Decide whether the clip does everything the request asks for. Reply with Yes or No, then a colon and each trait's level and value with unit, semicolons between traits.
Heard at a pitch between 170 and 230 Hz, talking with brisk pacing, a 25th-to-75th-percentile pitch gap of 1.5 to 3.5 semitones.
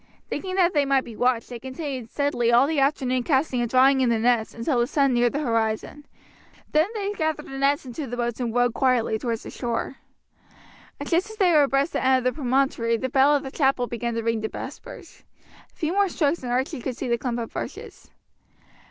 No: very high, 260 Hz; fast, 220 wpm; average, 3.2 semitones